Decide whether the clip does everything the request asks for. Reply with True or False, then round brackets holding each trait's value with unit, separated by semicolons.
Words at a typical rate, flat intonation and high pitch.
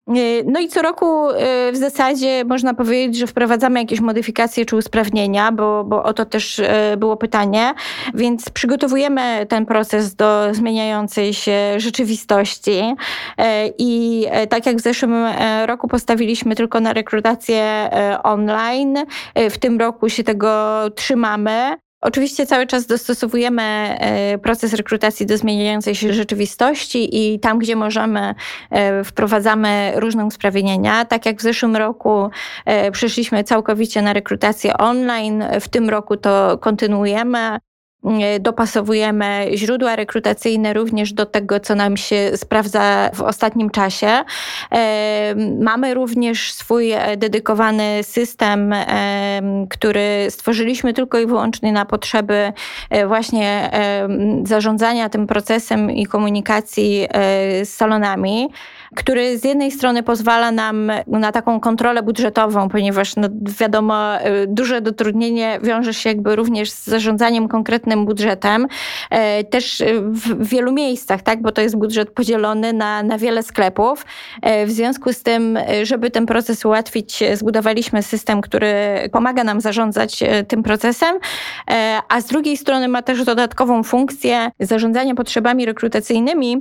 True (120 wpm; 2.0 semitones; 225 Hz)